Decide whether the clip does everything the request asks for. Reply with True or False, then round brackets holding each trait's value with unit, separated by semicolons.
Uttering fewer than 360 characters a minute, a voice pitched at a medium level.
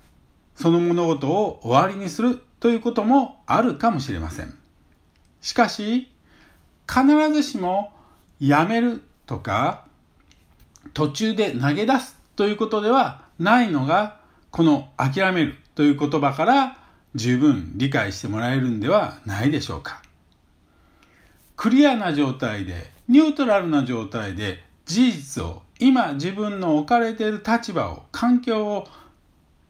True (255 characters per minute; 175 Hz)